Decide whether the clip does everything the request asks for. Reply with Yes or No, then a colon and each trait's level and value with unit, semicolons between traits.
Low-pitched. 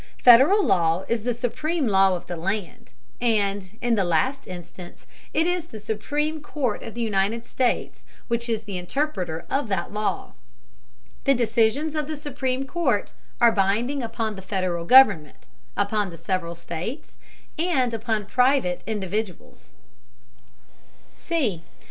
No: high, 220 Hz